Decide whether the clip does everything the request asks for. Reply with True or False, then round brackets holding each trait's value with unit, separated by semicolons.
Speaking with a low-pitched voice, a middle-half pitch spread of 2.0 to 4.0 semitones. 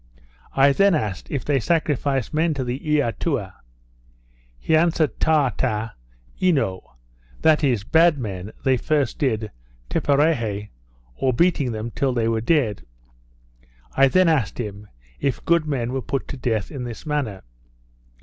False (130 Hz; 5.5 semitones)